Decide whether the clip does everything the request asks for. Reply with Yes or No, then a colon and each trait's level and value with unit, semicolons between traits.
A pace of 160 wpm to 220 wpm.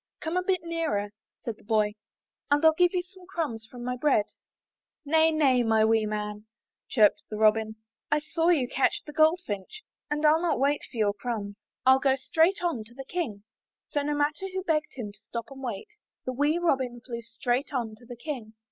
Yes: average, 200 wpm